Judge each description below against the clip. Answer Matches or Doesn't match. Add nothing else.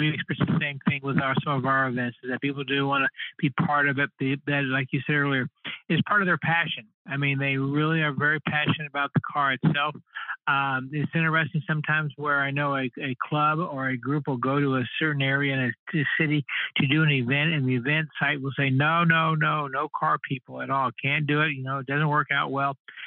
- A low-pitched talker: Doesn't match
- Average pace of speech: Doesn't match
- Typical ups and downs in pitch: Doesn't match